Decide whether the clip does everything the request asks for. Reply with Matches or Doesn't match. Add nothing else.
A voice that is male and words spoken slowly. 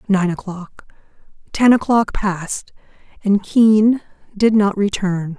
Doesn't match